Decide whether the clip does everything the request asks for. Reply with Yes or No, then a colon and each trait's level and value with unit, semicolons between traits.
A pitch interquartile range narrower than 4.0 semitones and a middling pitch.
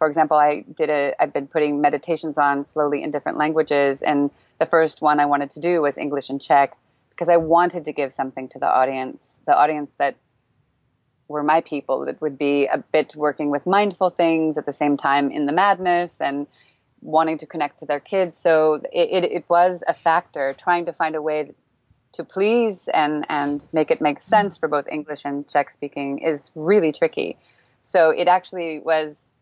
Yes: narrow, 2.4 semitones; medium, 150 Hz